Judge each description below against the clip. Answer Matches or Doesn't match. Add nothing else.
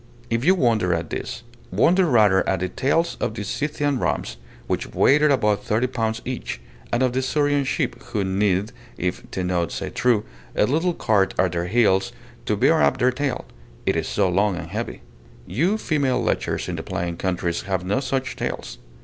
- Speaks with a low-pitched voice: Matches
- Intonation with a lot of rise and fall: Matches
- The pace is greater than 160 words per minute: Matches